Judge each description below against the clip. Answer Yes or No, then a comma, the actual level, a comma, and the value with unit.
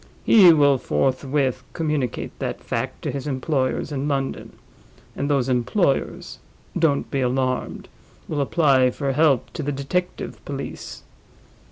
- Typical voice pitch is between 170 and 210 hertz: No, medium, 140 Hz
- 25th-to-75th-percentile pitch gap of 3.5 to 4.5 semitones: No, narrow, 2.4 semitones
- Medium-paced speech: No, slow, 130 wpm